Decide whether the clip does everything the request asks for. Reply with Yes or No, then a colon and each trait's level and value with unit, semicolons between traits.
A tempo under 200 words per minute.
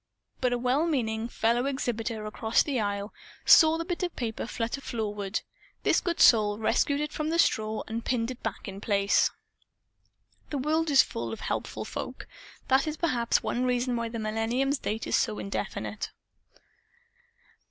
Yes: average, 170 wpm